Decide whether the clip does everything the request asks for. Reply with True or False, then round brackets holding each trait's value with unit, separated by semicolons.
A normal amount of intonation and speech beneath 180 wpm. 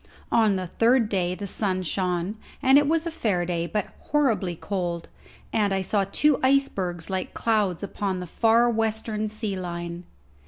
True (3.9 semitones; 165 wpm)